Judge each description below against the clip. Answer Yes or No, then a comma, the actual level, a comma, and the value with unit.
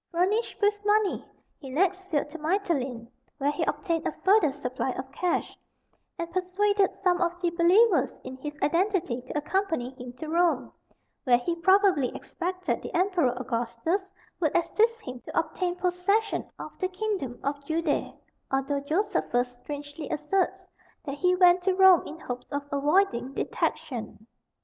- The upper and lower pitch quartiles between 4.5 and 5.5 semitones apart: Yes, average, 5.2 semitones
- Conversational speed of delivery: Yes, average, 150 wpm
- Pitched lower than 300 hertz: No, very high, 335 Hz